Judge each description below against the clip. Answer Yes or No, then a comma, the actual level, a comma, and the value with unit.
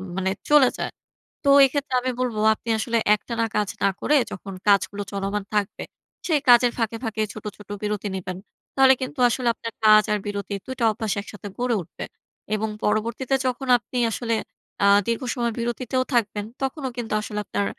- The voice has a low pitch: No, high, 230 Hz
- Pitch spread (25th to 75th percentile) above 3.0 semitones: Yes, average, 3.5 semitones